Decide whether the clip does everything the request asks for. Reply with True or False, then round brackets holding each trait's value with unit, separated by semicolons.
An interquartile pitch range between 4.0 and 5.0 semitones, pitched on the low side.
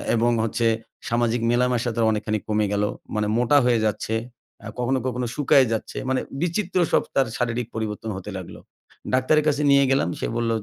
False (2.9 semitones; 120 Hz)